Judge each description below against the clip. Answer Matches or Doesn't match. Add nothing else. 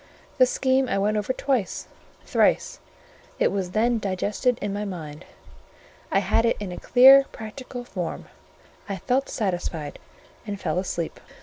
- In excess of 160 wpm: Doesn't match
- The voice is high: Matches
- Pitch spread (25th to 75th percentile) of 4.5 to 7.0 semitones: Matches